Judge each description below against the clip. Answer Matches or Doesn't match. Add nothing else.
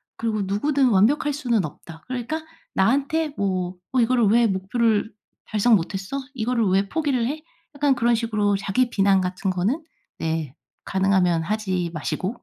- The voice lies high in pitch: Matches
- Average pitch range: Matches